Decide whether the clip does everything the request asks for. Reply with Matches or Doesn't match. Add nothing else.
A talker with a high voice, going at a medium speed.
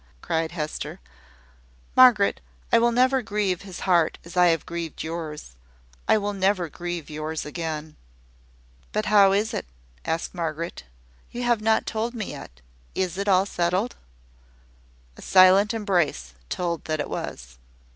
Doesn't match